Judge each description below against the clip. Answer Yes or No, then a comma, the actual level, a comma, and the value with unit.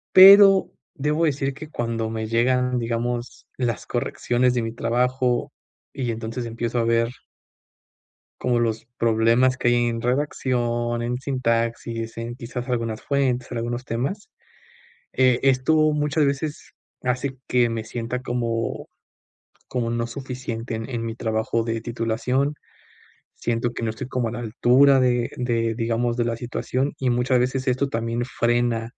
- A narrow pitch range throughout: Yes, narrow, 1.8 semitones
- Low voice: Yes, low, 120 Hz